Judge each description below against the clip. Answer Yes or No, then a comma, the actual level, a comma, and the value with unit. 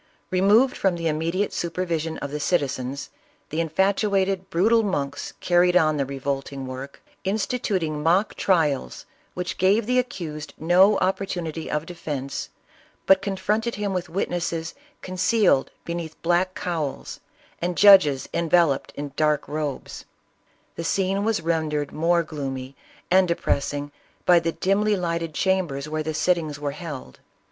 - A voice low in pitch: No, medium, 170 Hz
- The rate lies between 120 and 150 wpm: Yes, average, 140 wpm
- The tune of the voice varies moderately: Yes, average, 4.1 semitones